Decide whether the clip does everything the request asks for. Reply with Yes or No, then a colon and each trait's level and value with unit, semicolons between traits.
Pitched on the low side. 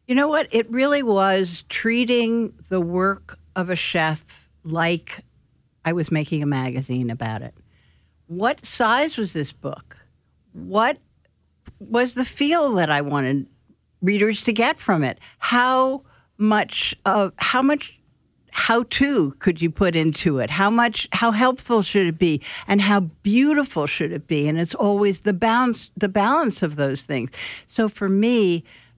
No: high, 195 Hz